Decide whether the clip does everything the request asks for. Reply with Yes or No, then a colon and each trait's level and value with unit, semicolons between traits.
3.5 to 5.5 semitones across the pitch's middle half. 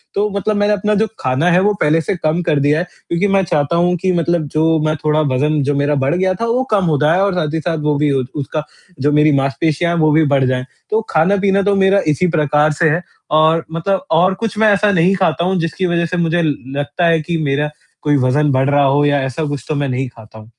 Yes: average, 3.9 semitones